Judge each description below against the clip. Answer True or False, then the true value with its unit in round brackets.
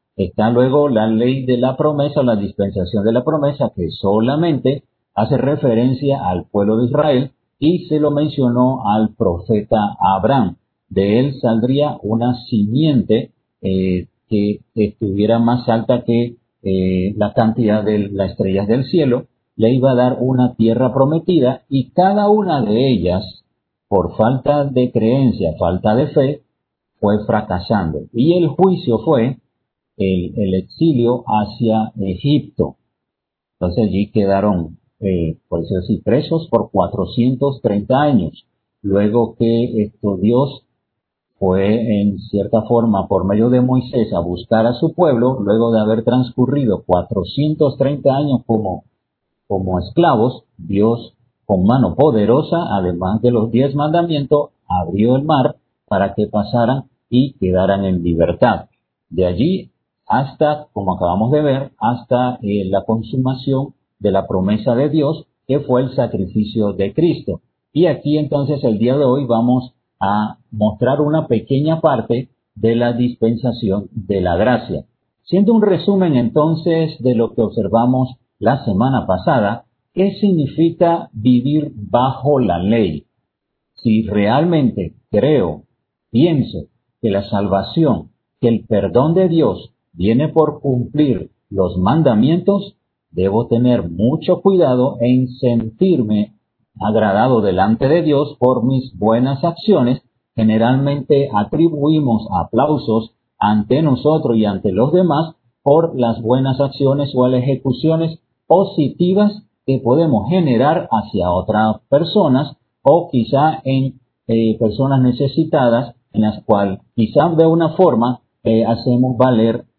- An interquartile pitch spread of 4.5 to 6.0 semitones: True (4.8 semitones)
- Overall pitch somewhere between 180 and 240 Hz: False (120 Hz)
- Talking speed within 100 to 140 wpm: True (130 wpm)